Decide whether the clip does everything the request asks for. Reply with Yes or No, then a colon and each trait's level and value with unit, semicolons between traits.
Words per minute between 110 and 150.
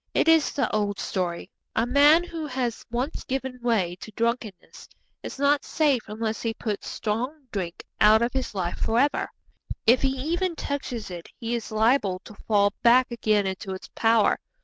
No: average, 175 wpm